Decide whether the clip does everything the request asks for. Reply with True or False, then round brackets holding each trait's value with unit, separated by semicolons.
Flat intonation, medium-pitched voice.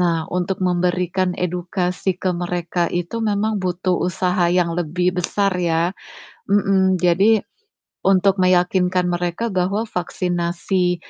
True (1.2 semitones; 180 Hz)